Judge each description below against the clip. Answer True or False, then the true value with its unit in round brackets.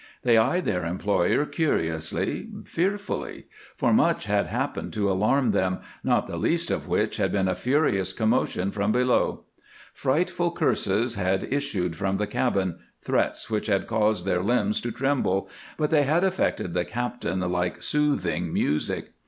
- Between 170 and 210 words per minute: False (155 wpm)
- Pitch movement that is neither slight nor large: False (6.6 semitones)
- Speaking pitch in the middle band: False (105 Hz)